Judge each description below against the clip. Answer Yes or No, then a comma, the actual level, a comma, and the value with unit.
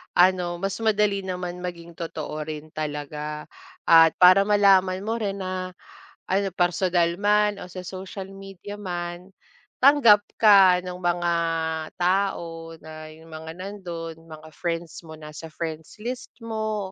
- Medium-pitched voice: Yes, medium, 180 Hz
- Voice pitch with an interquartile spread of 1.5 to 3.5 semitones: Yes, average, 3.1 semitones